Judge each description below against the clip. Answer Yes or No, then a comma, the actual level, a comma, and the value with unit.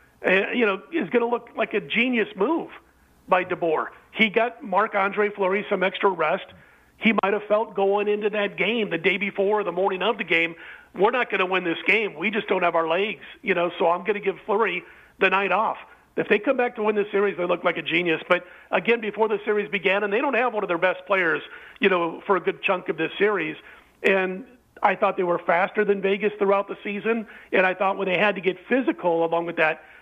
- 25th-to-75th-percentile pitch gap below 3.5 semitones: Yes, narrow, 2.5 semitones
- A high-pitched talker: Yes, high, 200 Hz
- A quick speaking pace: Yes, fast, 240 wpm